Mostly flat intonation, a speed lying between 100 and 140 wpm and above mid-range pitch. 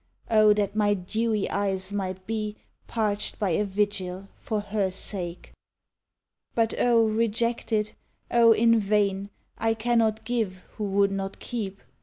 Yes: narrow, 2.3 semitones; slow, 135 wpm; high, 210 Hz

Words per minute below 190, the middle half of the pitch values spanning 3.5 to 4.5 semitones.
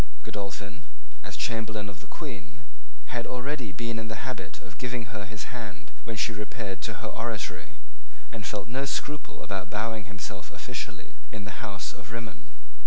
No: average, 170 wpm; average, 2.8 semitones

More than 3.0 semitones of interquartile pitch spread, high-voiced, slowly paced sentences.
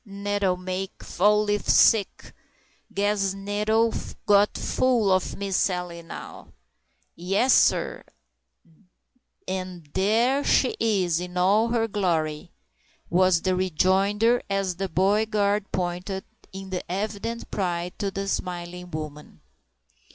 No: narrow, 2.5 semitones; high, 195 Hz; slow, 115 wpm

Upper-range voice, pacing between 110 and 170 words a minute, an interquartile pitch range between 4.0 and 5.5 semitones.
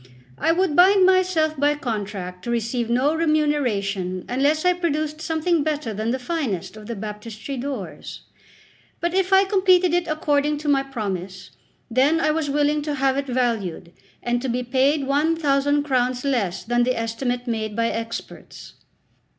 Yes: very high, 275 Hz; average, 165 wpm; average, 5.2 semitones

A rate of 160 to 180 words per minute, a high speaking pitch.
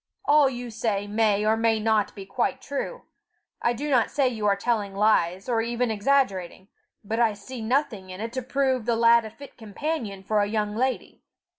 No: average, 195 wpm; high, 225 Hz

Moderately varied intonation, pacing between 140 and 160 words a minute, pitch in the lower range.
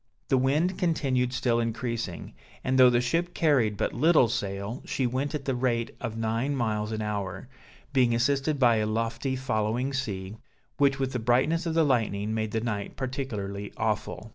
No: average, 3.6 semitones; average, 175 wpm; low, 120 Hz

